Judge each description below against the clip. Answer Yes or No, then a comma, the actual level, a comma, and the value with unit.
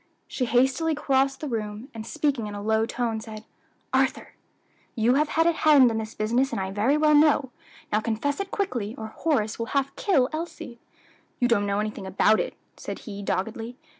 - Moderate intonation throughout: Yes, average, 4.8 semitones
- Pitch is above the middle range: Yes, high, 240 Hz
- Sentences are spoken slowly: No, average, 190 wpm